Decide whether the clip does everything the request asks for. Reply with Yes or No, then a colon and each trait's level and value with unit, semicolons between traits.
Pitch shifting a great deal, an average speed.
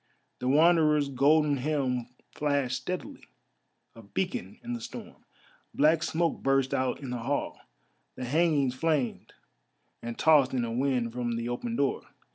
No: average, 4.0 semitones; average, 145 wpm